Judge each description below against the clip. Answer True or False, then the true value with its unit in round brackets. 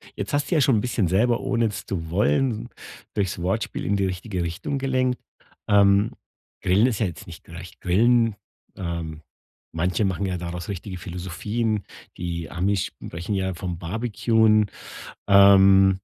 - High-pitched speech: False (100 Hz)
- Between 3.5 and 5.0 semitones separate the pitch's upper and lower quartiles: True (3.9 semitones)